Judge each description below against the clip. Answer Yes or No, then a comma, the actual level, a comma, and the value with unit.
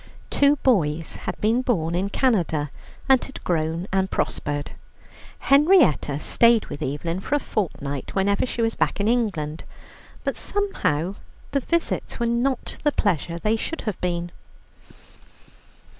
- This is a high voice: Yes, high, 200 Hz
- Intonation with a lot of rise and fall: Yes, wide, 7.2 semitones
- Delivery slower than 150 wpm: Yes, average, 140 wpm